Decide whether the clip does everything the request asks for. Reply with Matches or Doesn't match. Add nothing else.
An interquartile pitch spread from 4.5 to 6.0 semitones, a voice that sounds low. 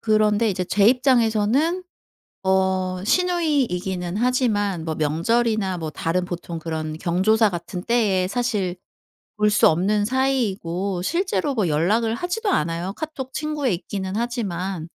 Doesn't match